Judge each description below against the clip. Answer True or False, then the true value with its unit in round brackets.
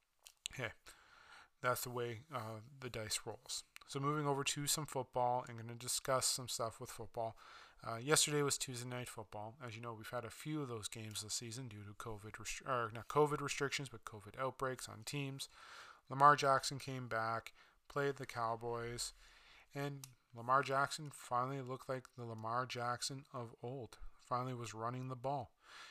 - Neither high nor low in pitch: False (125 Hz)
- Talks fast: False (180 wpm)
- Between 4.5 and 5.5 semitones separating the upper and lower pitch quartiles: False (3.1 semitones)